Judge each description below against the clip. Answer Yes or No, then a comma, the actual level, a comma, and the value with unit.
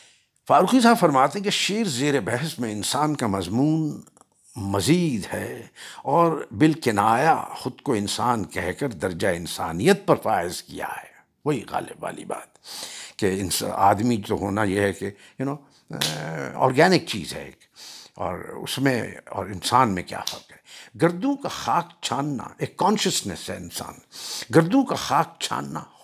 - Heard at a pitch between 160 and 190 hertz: No, low, 135 Hz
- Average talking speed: Yes, average, 155 wpm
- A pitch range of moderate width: No, wide, 8.5 semitones